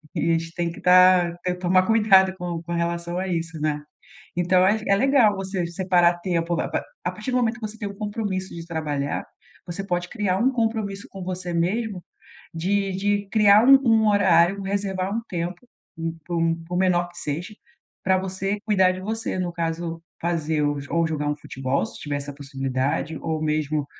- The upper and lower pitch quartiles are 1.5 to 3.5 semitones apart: Yes, average, 3.1 semitones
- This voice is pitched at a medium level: Yes, medium, 180 Hz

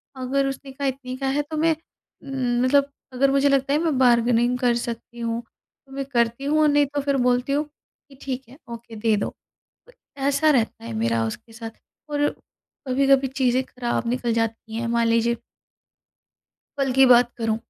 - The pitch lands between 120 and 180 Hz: No, very high, 255 Hz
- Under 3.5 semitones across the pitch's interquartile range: Yes, average, 2.8 semitones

